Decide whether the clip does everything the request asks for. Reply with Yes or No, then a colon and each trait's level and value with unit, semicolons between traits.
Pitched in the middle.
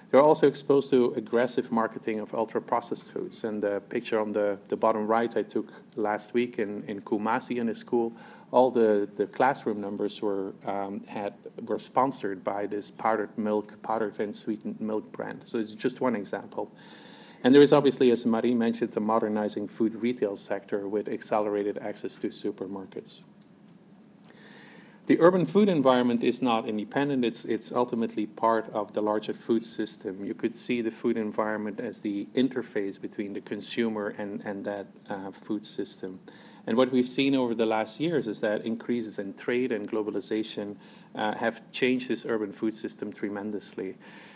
No: low, 115 Hz